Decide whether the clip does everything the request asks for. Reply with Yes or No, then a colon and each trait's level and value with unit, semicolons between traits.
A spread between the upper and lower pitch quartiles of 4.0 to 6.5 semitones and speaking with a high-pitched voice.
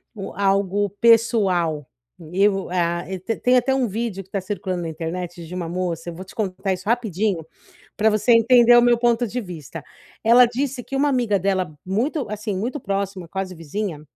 Yes: average, 4.4 semitones; high, 200 Hz